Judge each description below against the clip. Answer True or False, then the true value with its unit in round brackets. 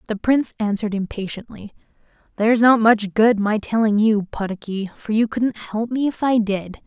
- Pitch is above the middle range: True (220 Hz)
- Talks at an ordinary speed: True (175 wpm)